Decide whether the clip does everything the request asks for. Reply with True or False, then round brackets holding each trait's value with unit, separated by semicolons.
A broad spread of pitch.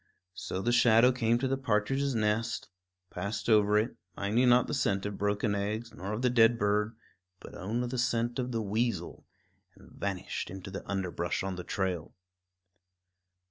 False (3.2 semitones)